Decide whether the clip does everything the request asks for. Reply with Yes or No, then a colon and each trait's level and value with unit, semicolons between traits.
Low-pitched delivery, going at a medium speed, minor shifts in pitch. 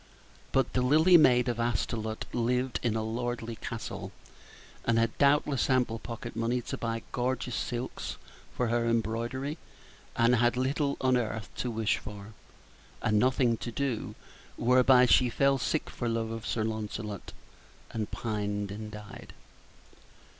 Yes: low, 120 Hz; average, 145 wpm; narrow, 2.2 semitones